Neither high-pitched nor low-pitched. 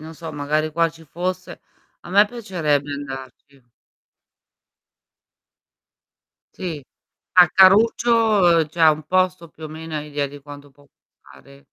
Yes: medium, 160 Hz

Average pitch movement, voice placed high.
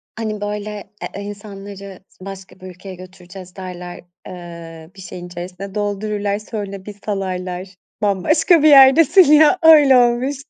Yes: average, 3.0 semitones; high, 200 Hz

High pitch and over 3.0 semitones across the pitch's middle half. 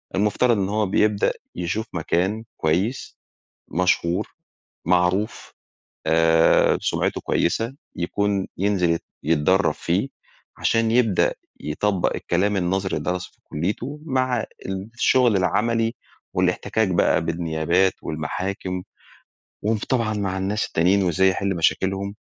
No: very low, 95 Hz; average, 3.5 semitones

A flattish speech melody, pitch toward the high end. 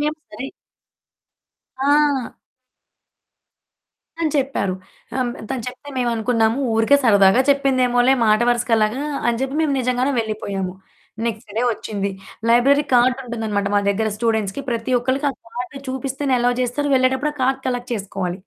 No: average, 3.2 semitones; high, 245 Hz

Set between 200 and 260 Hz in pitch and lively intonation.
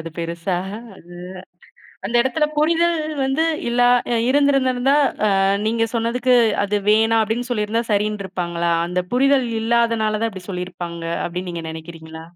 Yes: high, 220 Hz; wide, 5.7 semitones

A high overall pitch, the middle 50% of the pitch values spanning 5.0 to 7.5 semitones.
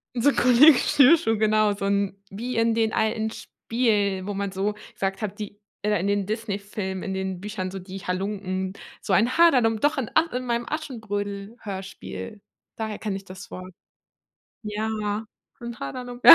No: high, 210 Hz; average, 2.8 semitones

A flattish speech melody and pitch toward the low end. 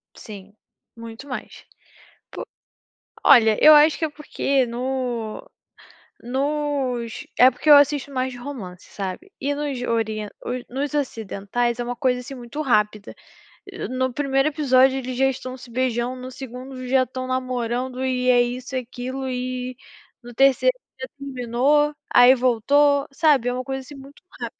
No: narrow, 2.1 semitones; very high, 255 Hz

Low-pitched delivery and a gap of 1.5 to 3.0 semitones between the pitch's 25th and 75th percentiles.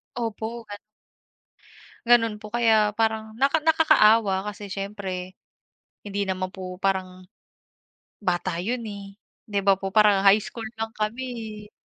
No: high, 210 Hz; narrow, 2.5 semitones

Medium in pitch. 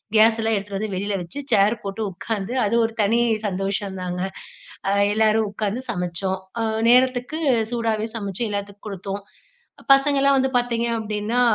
No: high, 215 Hz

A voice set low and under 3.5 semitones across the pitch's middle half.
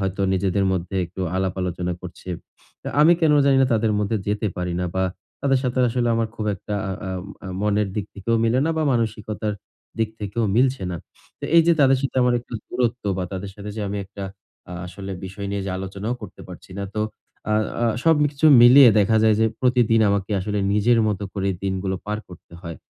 No: low, 105 Hz; average, 3.9 semitones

